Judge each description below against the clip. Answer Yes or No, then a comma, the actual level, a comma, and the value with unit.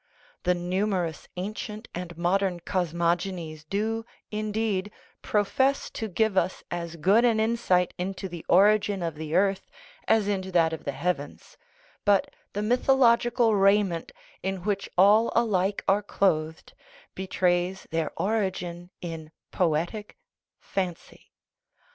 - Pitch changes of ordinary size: Yes, average, 3.3 semitones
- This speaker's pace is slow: Yes, slow, 120 wpm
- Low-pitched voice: No, high, 190 Hz